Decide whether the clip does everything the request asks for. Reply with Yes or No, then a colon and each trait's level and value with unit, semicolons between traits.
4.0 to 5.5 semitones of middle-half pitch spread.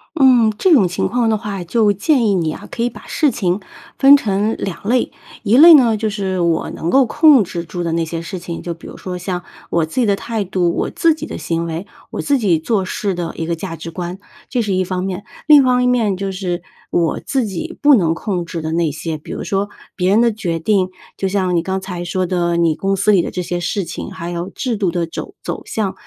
Yes: average, 4.4 semitones